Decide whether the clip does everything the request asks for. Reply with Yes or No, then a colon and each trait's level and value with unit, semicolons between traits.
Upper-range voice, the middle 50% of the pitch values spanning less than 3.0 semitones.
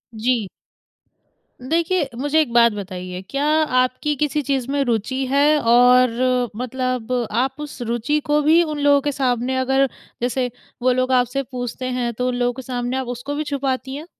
Yes: very high, 255 Hz; narrow, 2.5 semitones